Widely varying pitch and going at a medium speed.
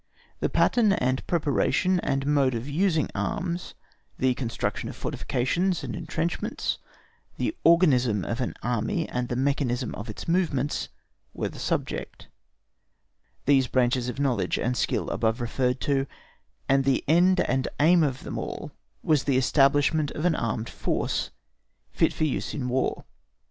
No: average, 4.3 semitones; average, 150 wpm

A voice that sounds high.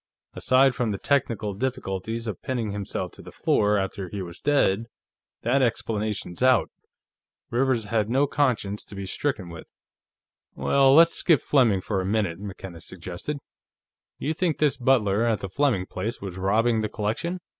No: low, 110 Hz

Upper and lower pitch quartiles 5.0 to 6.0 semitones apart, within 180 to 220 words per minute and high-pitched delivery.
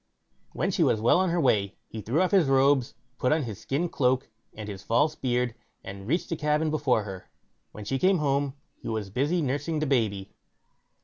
No: wide, 5.6 semitones; average, 200 wpm; low, 135 Hz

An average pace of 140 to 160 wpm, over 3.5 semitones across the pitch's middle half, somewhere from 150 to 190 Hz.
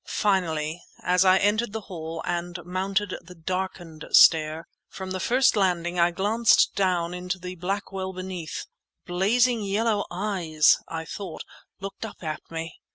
No: average, 150 wpm; narrow, 2.6 semitones; medium, 185 Hz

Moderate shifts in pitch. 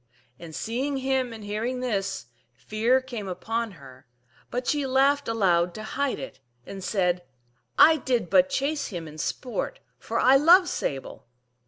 No: wide, 5.8 semitones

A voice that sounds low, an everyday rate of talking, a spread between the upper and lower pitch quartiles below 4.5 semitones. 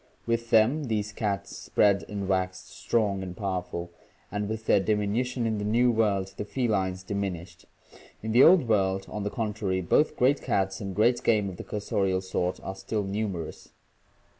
Yes: low, 105 Hz; average, 170 wpm; narrow, 2.6 semitones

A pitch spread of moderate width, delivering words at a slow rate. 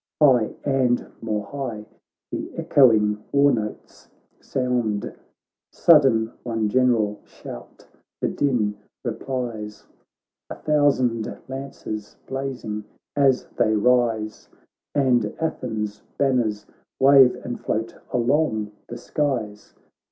Yes: average, 3.8 semitones; slow, 95 wpm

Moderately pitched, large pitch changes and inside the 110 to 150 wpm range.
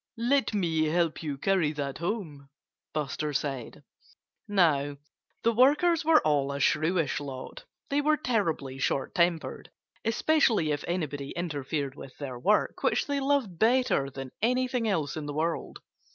Yes: medium, 165 Hz; wide, 8.0 semitones; average, 145 wpm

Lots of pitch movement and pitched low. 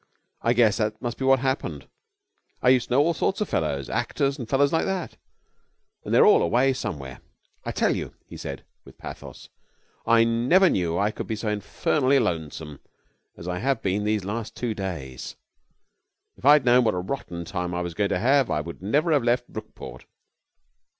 Yes: wide, 6.7 semitones; low, 115 Hz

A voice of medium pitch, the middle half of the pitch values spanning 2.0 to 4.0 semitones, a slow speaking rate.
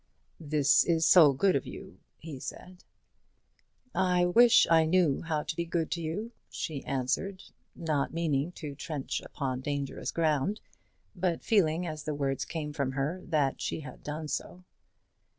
No: medium, 155 Hz; average, 3.5 semitones; average, 155 wpm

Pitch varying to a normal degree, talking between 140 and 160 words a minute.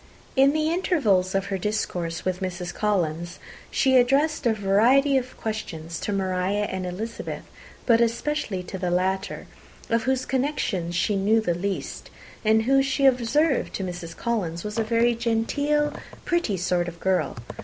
No: wide, 5.8 semitones; average, 155 wpm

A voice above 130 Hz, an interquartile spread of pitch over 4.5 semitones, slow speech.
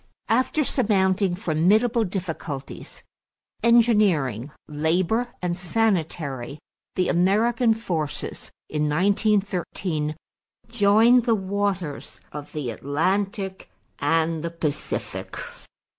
Yes: medium, 185 Hz; wide, 5.5 semitones; slow, 85 wpm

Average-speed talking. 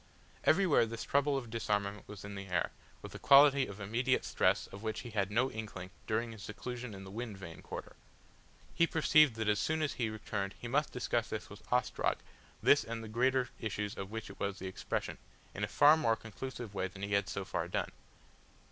No: fast, 210 wpm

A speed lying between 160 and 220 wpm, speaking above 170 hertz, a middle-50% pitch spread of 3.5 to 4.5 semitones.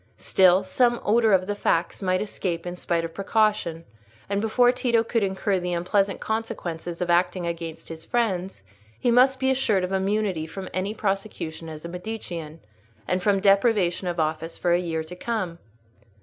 Yes: average, 175 wpm; medium, 185 Hz; average, 3.9 semitones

